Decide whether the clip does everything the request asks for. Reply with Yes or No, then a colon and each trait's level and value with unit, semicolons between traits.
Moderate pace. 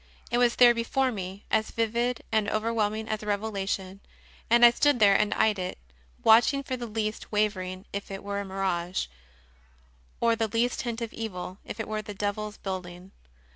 Yes: average, 195 wpm